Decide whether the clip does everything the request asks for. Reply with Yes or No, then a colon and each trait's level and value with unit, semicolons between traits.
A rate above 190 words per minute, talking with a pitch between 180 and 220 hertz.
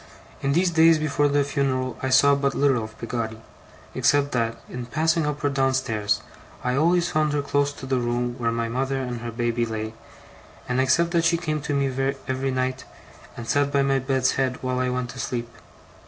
No: fast, 205 wpm; low, 135 Hz